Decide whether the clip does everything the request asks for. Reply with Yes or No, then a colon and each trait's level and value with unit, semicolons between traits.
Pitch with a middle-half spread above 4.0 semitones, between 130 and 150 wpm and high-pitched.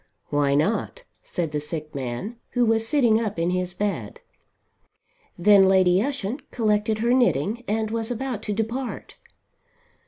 Yes: average, 4.5 semitones; average, 145 wpm; high, 210 Hz